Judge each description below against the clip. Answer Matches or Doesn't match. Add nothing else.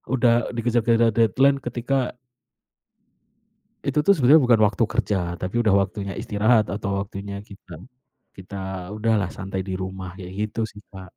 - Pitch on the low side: Matches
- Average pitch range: Matches